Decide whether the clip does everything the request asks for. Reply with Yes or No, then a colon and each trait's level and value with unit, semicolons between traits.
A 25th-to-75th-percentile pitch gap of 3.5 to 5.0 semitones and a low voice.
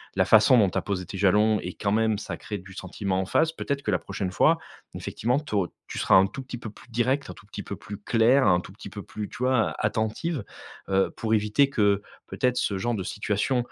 Yes: average, 3.9 semitones; low, 105 Hz